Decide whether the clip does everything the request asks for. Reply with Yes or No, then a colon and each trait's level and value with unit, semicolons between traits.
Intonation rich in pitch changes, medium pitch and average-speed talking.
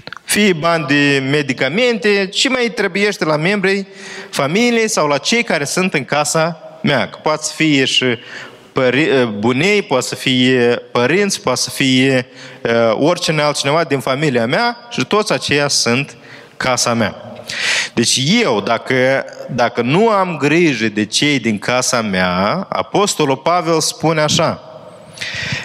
Yes: wide, 6.5 semitones; medium, 145 Hz; average, 135 wpm